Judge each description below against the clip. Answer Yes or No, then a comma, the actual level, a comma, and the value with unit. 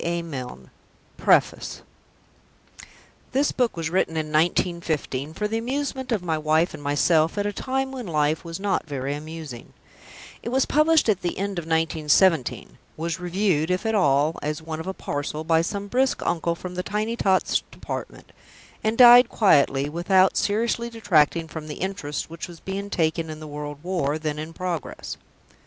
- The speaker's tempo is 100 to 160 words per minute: No, average, 170 wpm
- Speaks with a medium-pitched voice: Yes, medium, 170 Hz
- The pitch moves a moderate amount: Yes, average, 4.8 semitones